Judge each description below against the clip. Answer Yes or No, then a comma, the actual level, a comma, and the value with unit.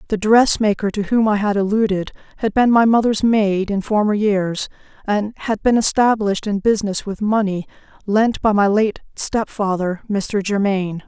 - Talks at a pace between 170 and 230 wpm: Yes, average, 175 wpm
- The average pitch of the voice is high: Yes, high, 205 Hz